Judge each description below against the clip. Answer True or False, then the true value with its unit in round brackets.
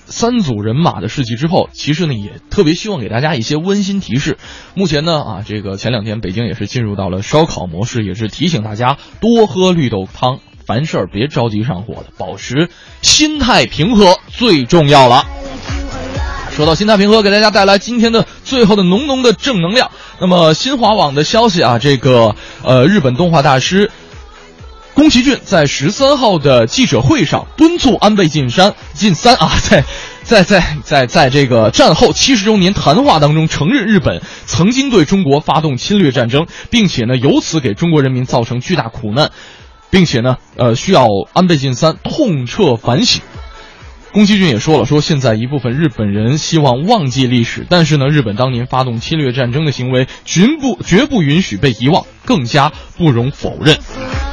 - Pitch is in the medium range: True (155 Hz)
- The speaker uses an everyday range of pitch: False (7.9 semitones)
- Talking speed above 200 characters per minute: True (280 characters per minute)